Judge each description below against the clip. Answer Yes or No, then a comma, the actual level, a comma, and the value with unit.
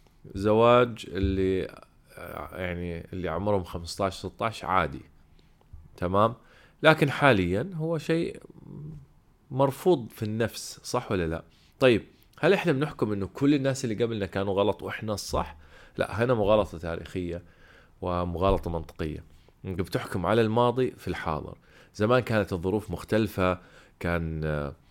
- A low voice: Yes, low, 100 Hz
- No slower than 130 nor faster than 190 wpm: No, average, 120 wpm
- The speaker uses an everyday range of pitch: No, wide, 5.7 semitones